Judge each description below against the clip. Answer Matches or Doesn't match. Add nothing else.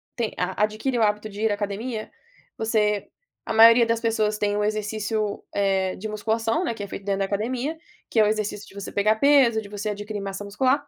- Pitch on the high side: Matches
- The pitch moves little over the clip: Matches